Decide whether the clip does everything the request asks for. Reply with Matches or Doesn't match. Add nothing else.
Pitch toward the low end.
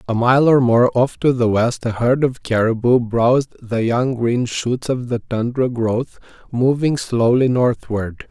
Matches